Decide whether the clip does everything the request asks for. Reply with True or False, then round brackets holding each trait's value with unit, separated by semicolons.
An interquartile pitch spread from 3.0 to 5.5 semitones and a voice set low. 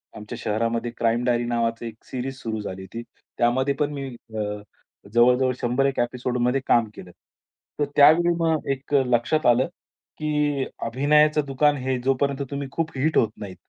True (3.4 semitones; 130 Hz)